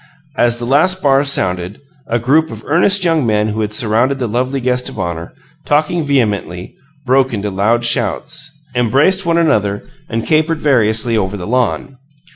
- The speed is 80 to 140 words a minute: No, average, 165 wpm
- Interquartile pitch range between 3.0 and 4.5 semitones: No, wide, 5.4 semitones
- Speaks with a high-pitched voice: No, low, 125 Hz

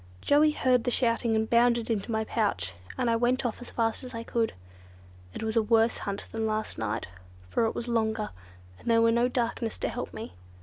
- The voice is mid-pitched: No, high, 230 Hz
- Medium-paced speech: No, fast, 215 wpm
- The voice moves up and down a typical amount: No, narrow, 1.5 semitones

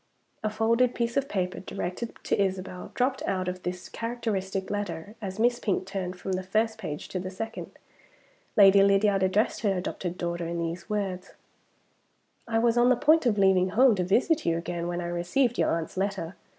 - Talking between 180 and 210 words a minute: Yes, average, 190 wpm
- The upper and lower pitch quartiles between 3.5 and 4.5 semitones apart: Yes, average, 3.8 semitones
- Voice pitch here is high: Yes, high, 195 Hz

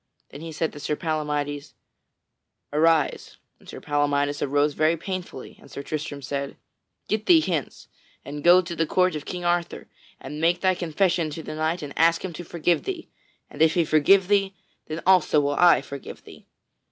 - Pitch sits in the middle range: Yes, medium, 160 Hz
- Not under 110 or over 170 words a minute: No, average, 185 wpm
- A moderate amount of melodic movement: Yes, average, 3.2 semitones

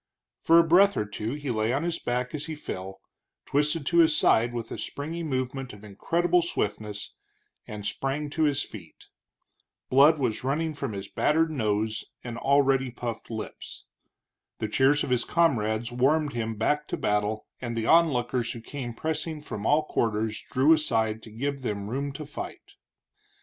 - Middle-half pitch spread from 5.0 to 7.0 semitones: Yes, average, 5.3 semitones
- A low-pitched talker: Yes, low, 130 Hz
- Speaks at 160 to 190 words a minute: Yes, average, 170 wpm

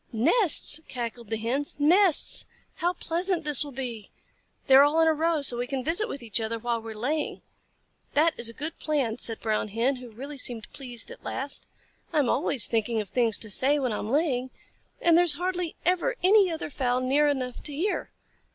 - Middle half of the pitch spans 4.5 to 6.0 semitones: Yes, average, 5.2 semitones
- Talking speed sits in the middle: No, fast, 215 wpm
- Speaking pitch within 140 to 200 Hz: No, very high, 275 Hz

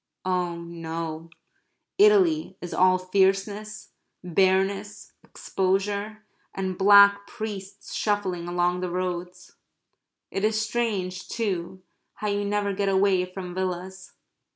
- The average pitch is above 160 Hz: Yes, high, 190 Hz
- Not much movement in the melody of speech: Yes, narrow, 2.1 semitones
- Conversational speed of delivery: No, slow, 105 wpm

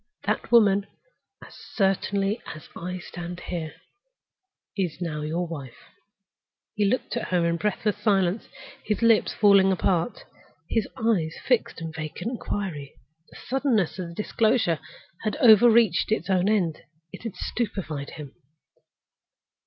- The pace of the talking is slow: Yes, slow, 125 wpm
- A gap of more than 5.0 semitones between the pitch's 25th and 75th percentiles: No, average, 4.5 semitones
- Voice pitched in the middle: No, high, 195 Hz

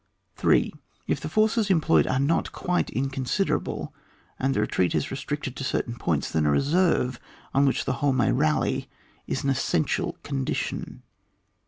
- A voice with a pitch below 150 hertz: Yes, low, 135 Hz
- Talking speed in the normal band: Yes, average, 165 wpm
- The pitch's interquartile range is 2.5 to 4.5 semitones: Yes, average, 3.9 semitones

